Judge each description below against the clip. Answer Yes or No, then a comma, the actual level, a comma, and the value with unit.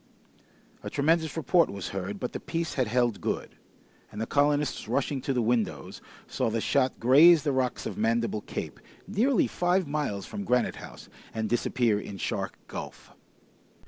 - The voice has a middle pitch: No, low, 130 Hz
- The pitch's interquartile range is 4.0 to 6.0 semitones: Yes, wide, 5.4 semitones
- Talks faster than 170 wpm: No, average, 165 wpm